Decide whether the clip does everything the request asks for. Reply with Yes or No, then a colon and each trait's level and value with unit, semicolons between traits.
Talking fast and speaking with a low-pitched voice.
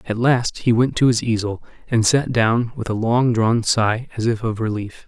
Yes: fast, 225 wpm; low, 115 Hz